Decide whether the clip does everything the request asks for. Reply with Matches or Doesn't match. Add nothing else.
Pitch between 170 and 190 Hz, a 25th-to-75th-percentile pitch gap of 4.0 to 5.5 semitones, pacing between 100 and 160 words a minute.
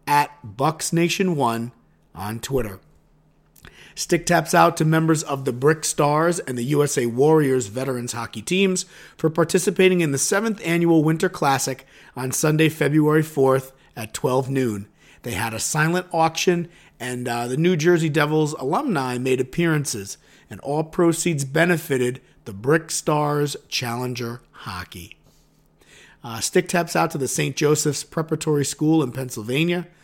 Doesn't match